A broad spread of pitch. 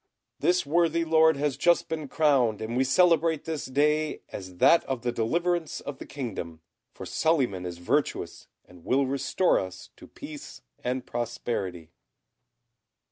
Yes: wide, 6.0 semitones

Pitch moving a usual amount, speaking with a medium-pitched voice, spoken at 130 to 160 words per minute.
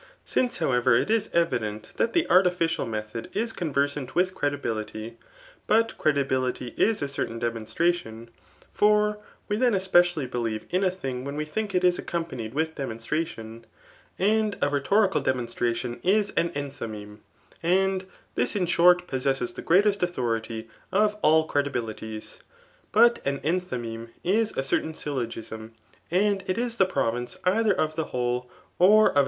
No: wide, 7.7 semitones; medium, 155 Hz; average, 140 wpm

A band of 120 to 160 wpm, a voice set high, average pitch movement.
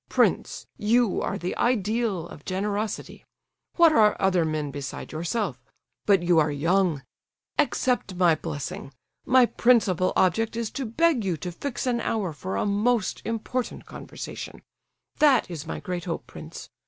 No: average, 140 wpm; high, 195 Hz; wide, 5.8 semitones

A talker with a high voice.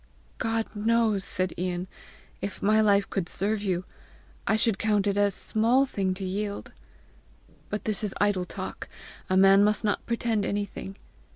Yes: high, 205 Hz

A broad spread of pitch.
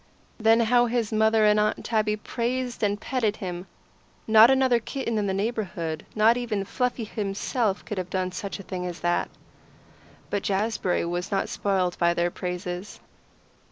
No: average, 3.7 semitones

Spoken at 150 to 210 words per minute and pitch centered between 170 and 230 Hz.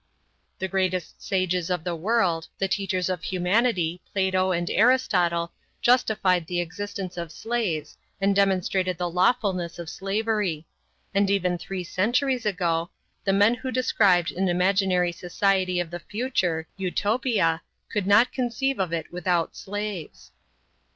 No: slow, 135 wpm; medium, 185 Hz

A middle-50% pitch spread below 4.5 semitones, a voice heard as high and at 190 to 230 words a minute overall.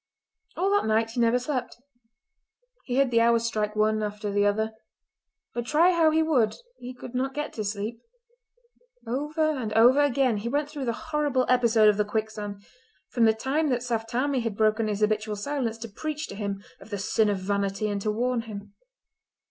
Yes: average, 3.8 semitones; high, 230 Hz; average, 195 wpm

